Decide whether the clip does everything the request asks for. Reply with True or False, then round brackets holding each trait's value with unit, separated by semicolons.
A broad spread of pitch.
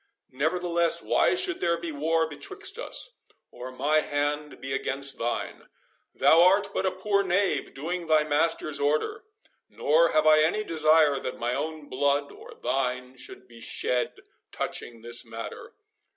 False (3.7 semitones)